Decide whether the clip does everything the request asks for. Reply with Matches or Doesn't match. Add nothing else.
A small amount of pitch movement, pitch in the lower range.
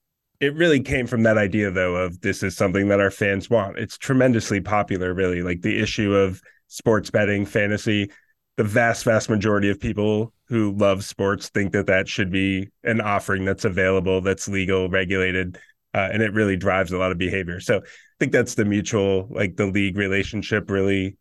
Matches